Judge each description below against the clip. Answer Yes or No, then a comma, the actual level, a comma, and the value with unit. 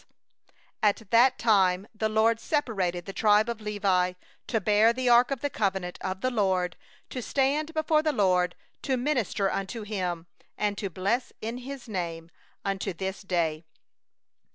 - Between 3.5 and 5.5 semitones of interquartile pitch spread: Yes, average, 4.4 semitones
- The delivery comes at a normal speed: Yes, average, 160 wpm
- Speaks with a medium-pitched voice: No, high, 210 Hz